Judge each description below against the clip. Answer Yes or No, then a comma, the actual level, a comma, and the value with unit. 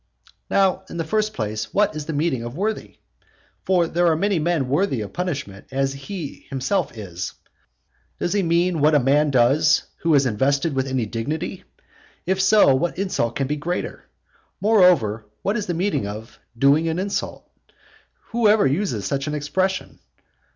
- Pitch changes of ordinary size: No, wide, 5.7 semitones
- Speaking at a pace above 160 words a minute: Yes, average, 170 wpm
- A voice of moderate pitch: Yes, medium, 155 Hz